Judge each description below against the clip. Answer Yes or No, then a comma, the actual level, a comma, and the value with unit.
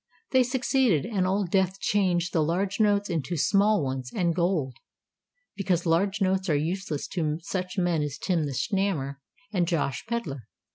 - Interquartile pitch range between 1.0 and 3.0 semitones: No, average, 4.1 semitones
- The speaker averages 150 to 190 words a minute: Yes, average, 160 wpm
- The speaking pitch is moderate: Yes, medium, 180 Hz